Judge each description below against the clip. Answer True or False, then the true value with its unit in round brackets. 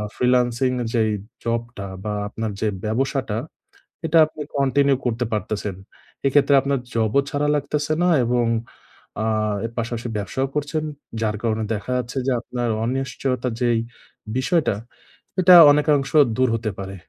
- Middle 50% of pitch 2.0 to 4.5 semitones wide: True (3.6 semitones)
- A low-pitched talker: True (125 Hz)